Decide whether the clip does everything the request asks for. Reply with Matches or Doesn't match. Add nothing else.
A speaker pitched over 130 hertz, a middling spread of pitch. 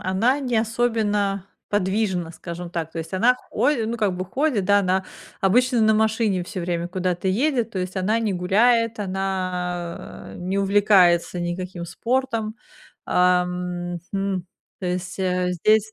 Matches